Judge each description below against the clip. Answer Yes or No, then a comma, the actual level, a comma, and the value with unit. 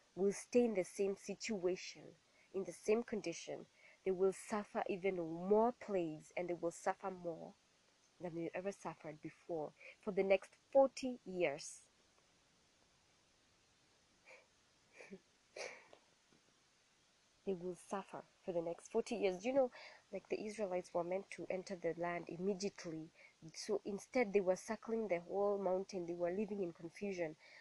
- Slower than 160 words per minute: Yes, average, 140 wpm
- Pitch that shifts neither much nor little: Yes, average, 3.2 semitones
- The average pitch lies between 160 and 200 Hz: Yes, high, 190 Hz